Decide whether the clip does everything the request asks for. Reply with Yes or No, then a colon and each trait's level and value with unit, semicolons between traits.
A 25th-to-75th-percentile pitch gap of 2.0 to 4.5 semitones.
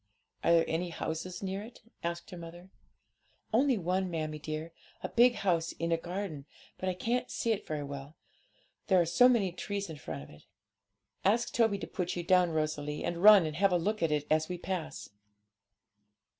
Yes: average, 3.7 semitones